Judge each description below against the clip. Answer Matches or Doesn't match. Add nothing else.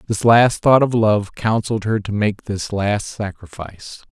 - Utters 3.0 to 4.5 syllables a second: Matches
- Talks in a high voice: Doesn't match